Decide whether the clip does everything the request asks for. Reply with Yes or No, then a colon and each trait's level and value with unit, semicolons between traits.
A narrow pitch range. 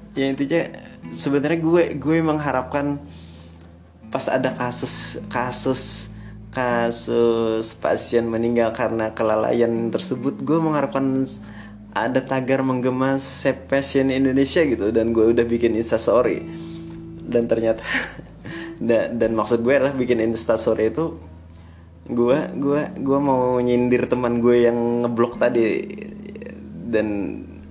No: average, 3.6 semitones